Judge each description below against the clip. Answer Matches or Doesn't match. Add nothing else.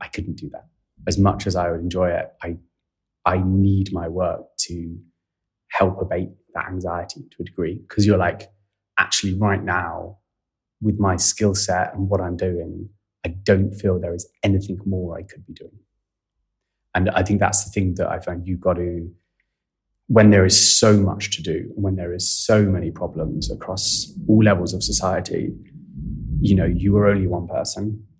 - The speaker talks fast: Doesn't match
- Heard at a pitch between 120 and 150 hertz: Doesn't match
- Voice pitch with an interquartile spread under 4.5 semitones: Matches